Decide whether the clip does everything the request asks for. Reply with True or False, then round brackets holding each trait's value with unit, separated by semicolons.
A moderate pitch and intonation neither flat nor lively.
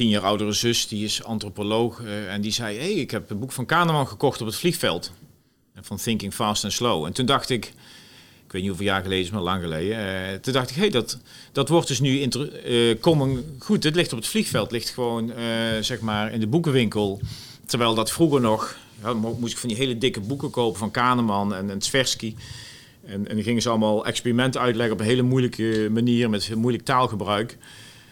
False (115 Hz; 3.2 semitones)